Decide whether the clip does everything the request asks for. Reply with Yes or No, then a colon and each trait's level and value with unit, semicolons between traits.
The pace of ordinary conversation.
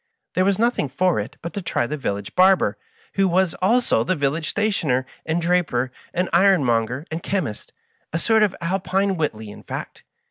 Yes: average, 185 wpm